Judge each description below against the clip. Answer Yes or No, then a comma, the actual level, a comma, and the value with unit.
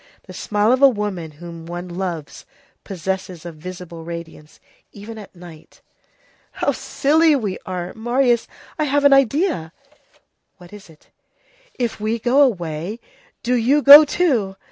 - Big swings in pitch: Yes, wide, 6.6 semitones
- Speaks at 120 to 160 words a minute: Yes, average, 145 wpm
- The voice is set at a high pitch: Yes, high, 205 Hz